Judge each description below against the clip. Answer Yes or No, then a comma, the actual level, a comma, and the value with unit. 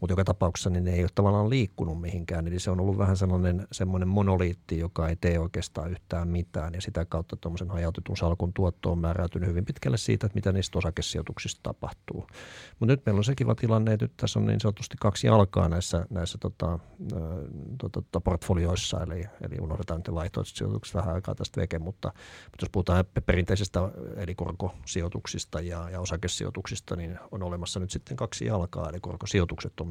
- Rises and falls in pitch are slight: No, average, 3.0 semitones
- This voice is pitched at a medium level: No, very low, 90 Hz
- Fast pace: Yes, fast, 185 wpm